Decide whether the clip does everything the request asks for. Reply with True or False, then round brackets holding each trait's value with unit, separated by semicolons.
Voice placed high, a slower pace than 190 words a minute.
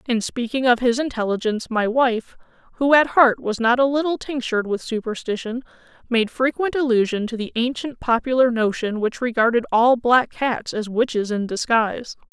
True (240 Hz; 165 wpm)